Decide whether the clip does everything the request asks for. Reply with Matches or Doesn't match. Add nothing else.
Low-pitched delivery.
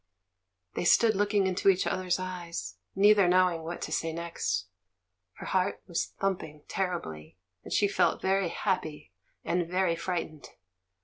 Doesn't match